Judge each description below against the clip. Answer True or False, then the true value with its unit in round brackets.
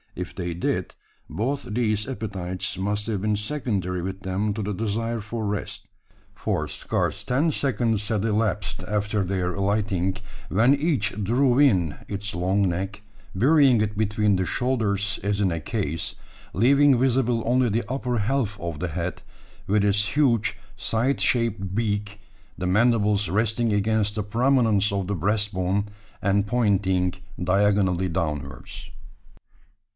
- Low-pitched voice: True (105 Hz)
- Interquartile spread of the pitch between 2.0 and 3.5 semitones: True (3.2 semitones)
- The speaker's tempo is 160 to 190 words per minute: False (140 wpm)